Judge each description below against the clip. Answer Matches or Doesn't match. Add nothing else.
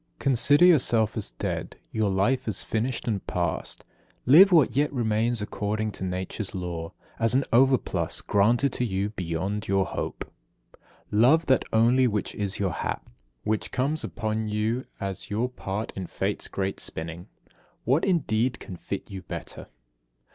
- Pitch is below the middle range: Matches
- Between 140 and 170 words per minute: Matches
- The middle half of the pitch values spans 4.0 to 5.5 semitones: Matches